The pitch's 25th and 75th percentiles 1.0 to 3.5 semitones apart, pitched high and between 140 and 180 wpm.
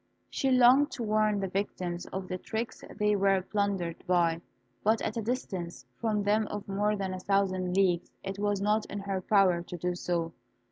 No: narrow, 2.5 semitones; high, 195 Hz; average, 190 wpm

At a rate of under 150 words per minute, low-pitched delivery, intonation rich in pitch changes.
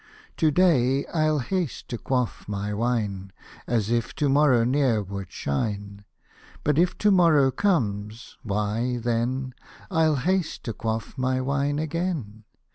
Yes: average, 140 wpm; low, 125 Hz; wide, 5.7 semitones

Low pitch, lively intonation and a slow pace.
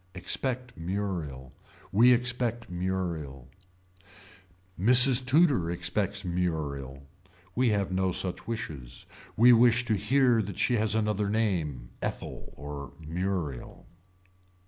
Yes: very low, 95 Hz; wide, 6.3 semitones; slow, 105 wpm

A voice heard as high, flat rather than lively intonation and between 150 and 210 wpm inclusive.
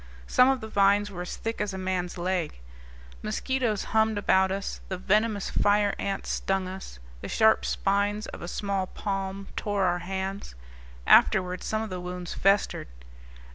Yes: high, 195 Hz; narrow, 1.9 semitones; average, 165 wpm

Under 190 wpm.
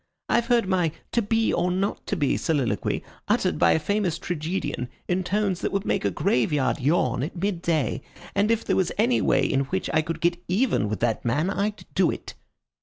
No: fast, 205 wpm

